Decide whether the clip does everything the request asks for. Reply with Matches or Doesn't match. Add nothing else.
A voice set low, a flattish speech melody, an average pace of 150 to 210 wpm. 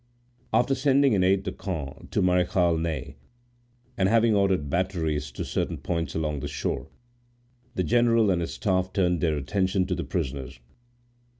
Doesn't match